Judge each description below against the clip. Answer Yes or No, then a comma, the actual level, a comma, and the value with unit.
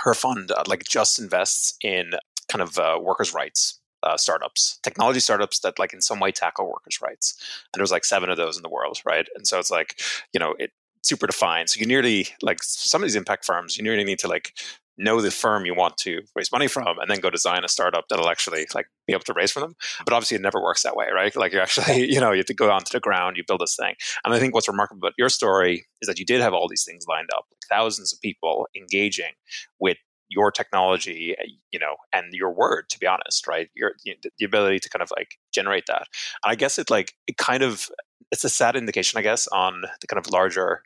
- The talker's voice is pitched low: Yes, low, 100 Hz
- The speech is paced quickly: Yes, fast, 245 wpm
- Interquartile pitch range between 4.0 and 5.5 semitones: Yes, average, 4.3 semitones